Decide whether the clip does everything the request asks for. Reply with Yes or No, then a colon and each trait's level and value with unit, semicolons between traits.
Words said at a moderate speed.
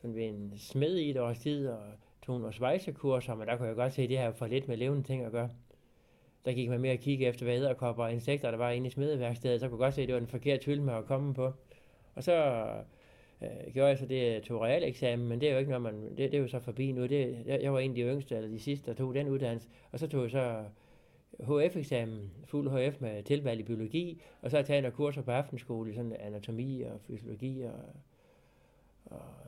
No: fast, 250 wpm